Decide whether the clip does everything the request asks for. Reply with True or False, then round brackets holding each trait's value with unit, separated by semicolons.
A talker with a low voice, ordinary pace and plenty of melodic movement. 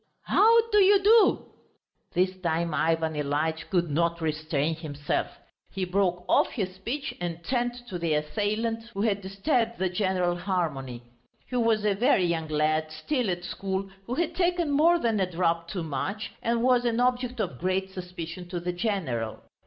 False (185 Hz; 170 wpm; 5.9 semitones)